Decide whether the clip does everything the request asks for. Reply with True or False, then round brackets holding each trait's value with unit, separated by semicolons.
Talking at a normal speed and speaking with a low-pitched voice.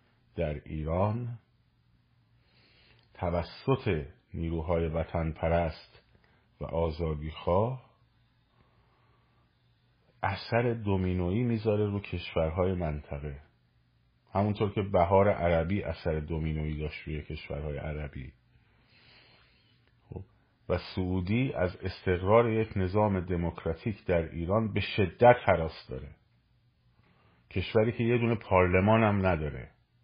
False (90 wpm; 95 Hz)